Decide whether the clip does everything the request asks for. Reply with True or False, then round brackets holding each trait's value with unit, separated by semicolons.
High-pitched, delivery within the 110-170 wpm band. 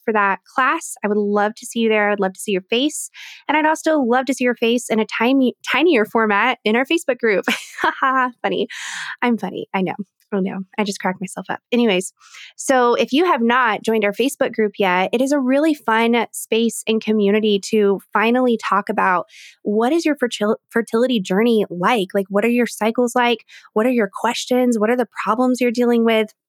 False (230 Hz; 205 wpm)